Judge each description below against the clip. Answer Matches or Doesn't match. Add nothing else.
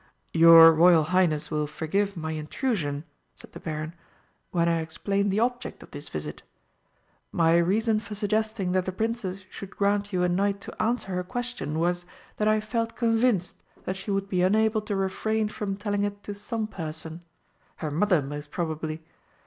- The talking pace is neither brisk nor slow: Matches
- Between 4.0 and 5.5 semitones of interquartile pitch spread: Matches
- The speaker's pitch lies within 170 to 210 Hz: Matches